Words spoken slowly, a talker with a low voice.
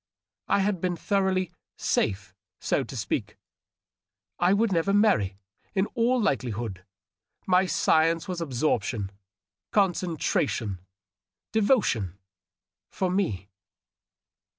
No: slow, 100 wpm; medium, 175 Hz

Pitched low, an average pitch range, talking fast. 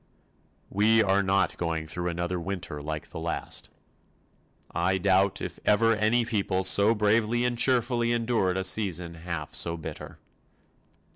No: very low, 95 Hz; average, 4.4 semitones; average, 140 wpm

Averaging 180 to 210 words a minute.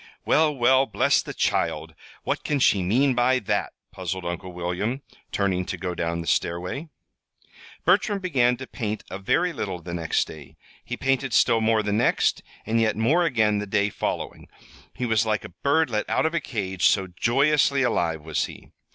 Yes: average, 185 wpm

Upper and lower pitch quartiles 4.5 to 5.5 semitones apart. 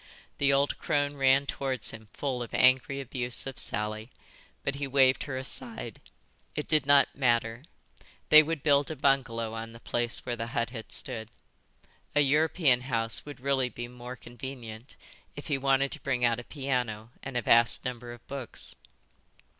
No: average, 2.8 semitones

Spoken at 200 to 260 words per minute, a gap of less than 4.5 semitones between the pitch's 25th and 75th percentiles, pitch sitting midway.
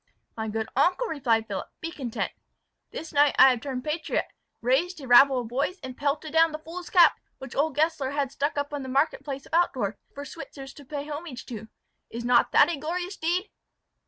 No: fast, 205 wpm; average, 4.0 semitones; very high, 285 Hz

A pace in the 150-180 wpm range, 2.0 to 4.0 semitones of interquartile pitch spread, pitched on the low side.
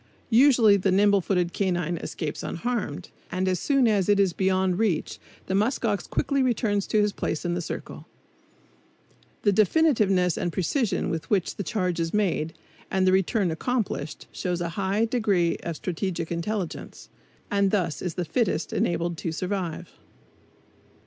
No: average, 155 wpm; average, 3.4 semitones; high, 190 Hz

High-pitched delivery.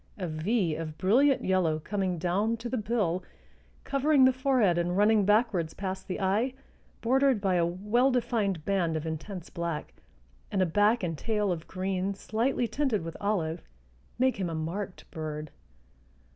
Yes: high, 195 Hz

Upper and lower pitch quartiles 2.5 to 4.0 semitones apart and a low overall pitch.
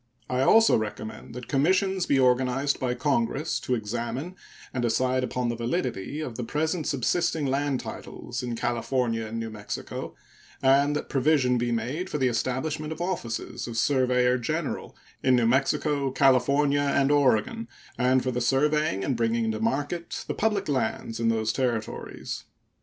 Yes: average, 3.7 semitones; low, 130 Hz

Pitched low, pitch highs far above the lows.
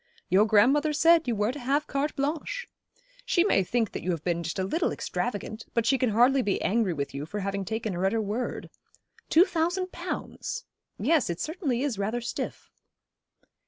No: high, 235 Hz; wide, 7.0 semitones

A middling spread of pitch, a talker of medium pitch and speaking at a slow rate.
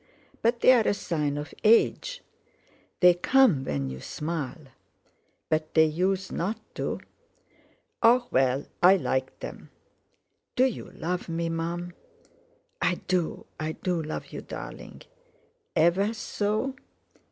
Yes: average, 5.0 semitones; medium, 175 Hz; slow, 115 wpm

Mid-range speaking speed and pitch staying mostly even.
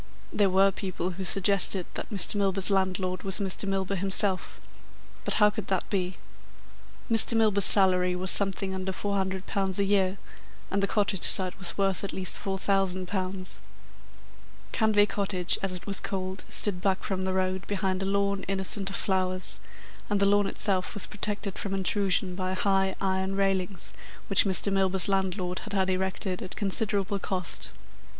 Yes: average, 160 wpm; narrow, 1.2 semitones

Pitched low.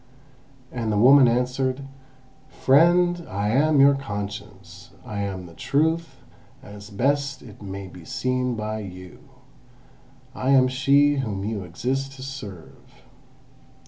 Yes: low, 125 Hz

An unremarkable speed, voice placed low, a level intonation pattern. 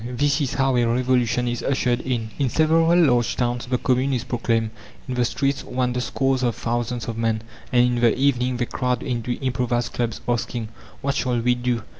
Yes: average, 195 wpm; low, 125 Hz; narrow, 1.5 semitones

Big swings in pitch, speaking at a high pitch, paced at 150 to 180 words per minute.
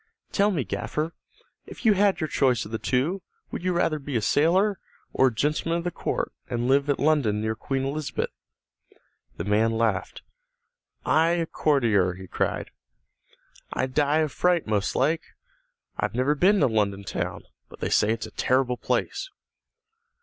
No: wide, 6.5 semitones; low, 135 Hz; average, 170 wpm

